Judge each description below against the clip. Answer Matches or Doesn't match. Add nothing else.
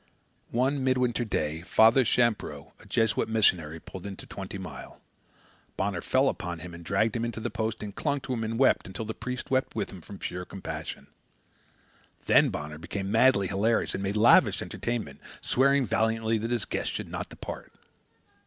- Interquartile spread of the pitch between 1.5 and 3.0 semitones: Doesn't match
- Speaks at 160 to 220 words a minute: Matches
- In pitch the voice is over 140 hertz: Doesn't match